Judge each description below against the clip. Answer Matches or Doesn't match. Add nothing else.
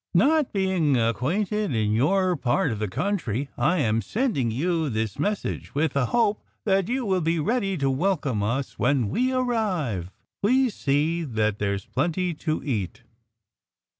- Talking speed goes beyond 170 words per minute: Doesn't match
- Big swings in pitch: Matches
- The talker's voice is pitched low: Doesn't match